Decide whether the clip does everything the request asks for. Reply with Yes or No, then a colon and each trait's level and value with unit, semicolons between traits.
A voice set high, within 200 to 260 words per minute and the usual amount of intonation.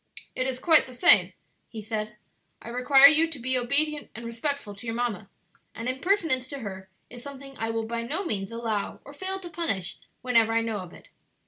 Yes: high, 245 Hz; fast, 205 wpm; average, 3.9 semitones